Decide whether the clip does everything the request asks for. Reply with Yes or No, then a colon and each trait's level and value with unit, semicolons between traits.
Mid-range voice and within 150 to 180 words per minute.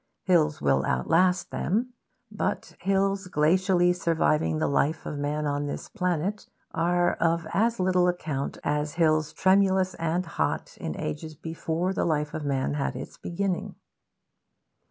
No: medium, 170 Hz; average, 140 wpm